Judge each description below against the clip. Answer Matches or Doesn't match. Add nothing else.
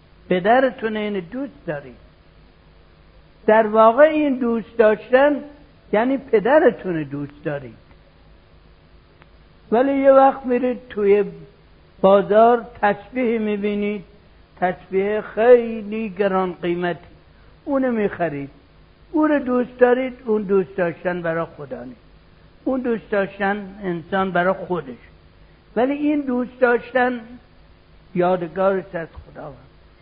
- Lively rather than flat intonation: Matches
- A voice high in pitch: Matches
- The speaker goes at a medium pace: Doesn't match